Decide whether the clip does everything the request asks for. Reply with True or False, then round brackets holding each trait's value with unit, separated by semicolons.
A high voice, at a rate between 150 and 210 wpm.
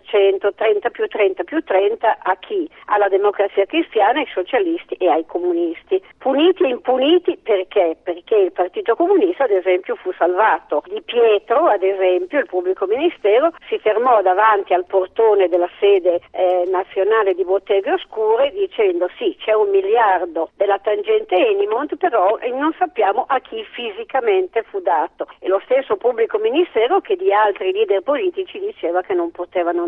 True (220 Hz; 155 wpm)